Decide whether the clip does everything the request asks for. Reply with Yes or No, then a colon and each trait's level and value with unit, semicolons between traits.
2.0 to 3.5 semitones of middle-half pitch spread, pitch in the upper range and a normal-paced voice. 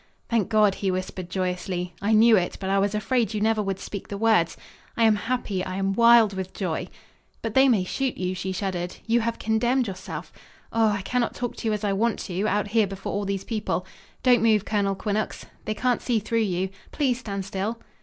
No: average, 3.0 semitones; high, 210 Hz; fast, 215 wpm